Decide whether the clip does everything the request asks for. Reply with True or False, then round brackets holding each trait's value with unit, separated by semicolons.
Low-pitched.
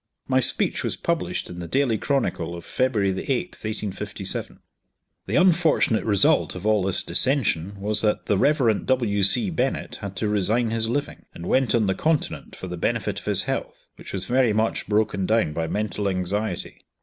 True (105 Hz)